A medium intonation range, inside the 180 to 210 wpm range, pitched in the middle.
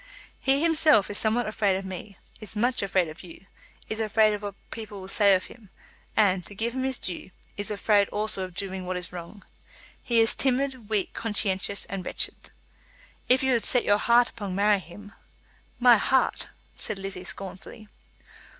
No: average, 3.2 semitones; average, 185 wpm; high, 205 Hz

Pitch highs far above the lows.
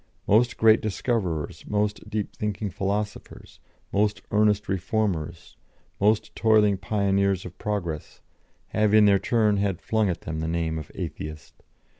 No: average, 2.8 semitones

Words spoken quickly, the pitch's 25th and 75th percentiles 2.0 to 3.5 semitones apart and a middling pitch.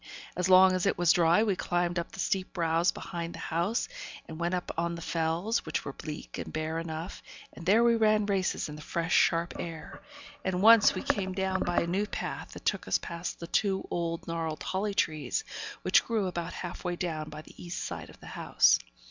Yes: fast, 215 wpm; narrow, 2.4 semitones; medium, 175 Hz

